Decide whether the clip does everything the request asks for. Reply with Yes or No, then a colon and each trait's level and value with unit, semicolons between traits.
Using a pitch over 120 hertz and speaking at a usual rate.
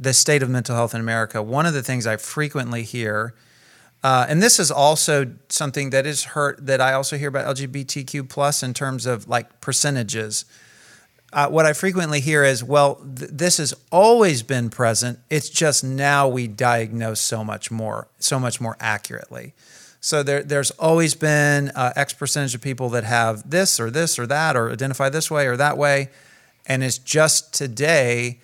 Yes: low, 135 Hz; average, 185 wpm